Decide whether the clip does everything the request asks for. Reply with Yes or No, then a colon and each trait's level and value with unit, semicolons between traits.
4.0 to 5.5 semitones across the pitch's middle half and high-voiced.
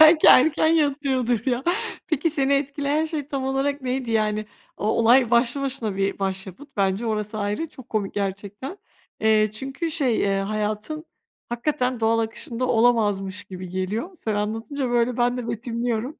Yes: average, 4.4 semitones; high, 240 Hz